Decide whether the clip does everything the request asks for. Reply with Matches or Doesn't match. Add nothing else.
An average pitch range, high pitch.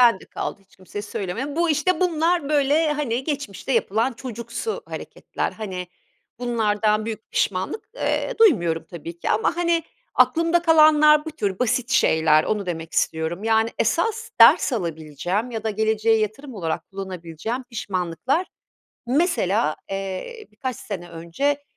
Doesn't match